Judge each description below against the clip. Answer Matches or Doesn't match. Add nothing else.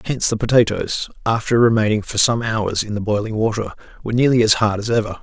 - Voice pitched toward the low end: Matches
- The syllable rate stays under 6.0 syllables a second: Doesn't match